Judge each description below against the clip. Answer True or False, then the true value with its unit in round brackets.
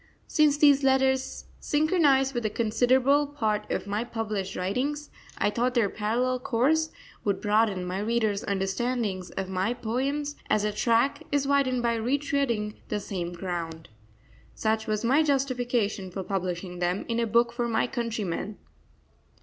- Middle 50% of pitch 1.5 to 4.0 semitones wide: False (4.5 semitones)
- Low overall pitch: False (235 Hz)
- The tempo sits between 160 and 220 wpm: False (150 wpm)